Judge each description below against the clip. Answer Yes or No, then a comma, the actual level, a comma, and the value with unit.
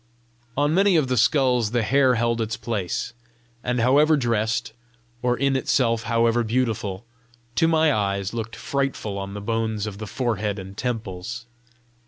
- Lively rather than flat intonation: No, average, 3.1 semitones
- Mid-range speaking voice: No, low, 115 Hz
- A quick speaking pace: No, average, 155 wpm